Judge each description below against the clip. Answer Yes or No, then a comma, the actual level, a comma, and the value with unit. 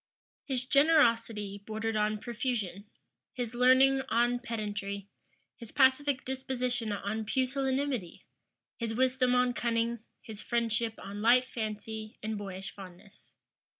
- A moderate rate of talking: No, slow, 115 wpm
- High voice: Yes, high, 230 Hz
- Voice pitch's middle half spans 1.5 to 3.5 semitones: Yes, average, 3.2 semitones